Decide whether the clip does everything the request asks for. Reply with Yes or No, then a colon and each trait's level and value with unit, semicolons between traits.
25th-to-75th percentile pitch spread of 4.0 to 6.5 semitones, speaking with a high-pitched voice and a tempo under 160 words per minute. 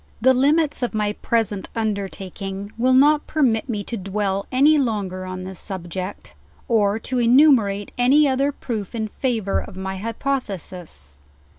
Yes: average, 4.9 semitones; high, 220 Hz; average, 150 wpm